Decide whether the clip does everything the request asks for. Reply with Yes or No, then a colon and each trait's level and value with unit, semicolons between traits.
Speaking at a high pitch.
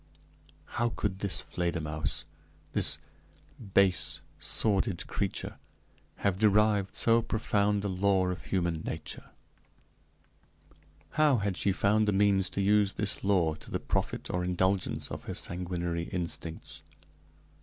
No: very low, 95 Hz